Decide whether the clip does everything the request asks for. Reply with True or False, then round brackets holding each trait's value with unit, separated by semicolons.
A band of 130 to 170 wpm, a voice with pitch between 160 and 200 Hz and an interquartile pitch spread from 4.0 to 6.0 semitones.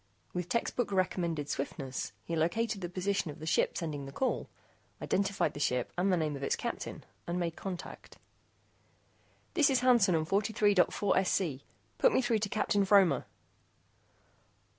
True (150 wpm; 185 Hz; 4.5 semitones)